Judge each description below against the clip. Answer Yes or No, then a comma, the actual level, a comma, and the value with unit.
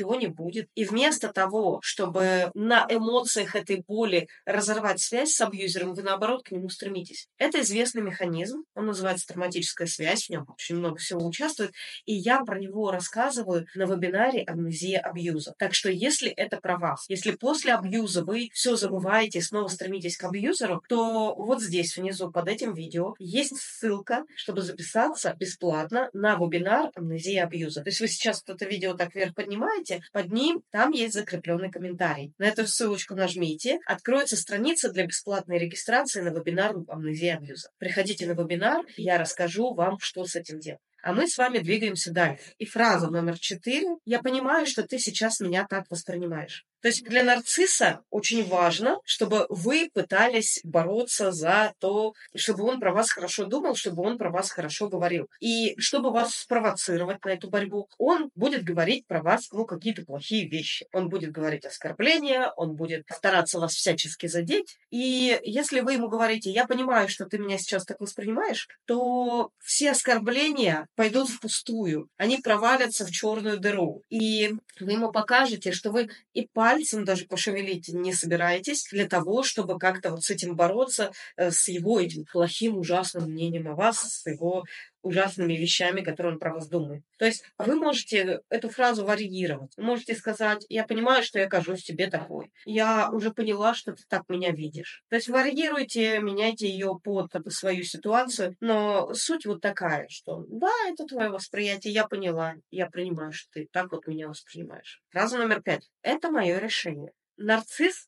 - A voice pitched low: No, high, 200 Hz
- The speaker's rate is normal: No, fast, 165 wpm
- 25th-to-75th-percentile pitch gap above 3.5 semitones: Yes, average, 4.3 semitones